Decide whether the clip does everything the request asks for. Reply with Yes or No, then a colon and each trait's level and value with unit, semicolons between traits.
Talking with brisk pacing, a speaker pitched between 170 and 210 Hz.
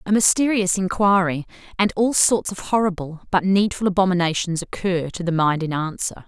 No: average, 165 wpm; medium, 185 Hz